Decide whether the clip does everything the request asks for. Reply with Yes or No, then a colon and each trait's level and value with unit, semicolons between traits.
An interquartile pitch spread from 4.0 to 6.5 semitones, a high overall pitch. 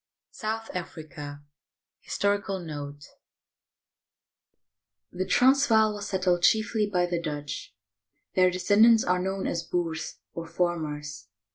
No: average, 4.4 semitones; medium, 180 Hz